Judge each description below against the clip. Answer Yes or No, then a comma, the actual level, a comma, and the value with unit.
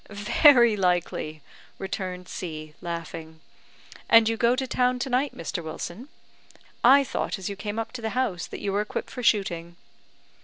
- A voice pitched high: Yes, high, 205 Hz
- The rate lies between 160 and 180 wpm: Yes, average, 165 wpm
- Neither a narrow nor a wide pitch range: No, wide, 6.0 semitones